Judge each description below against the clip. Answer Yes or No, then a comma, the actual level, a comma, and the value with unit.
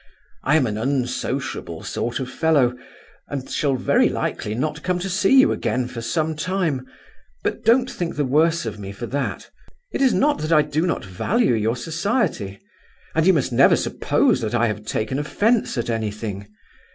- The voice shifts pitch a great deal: Yes, wide, 6.2 semitones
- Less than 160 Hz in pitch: Yes, medium, 140 Hz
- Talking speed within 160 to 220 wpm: Yes, average, 180 wpm